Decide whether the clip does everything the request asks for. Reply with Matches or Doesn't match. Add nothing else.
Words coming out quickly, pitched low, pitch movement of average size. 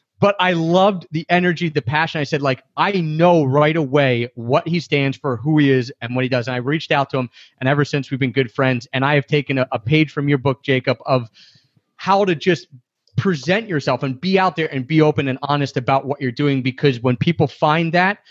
Doesn't match